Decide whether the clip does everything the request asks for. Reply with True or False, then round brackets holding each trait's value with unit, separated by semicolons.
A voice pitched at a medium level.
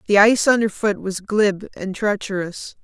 False (205 Hz)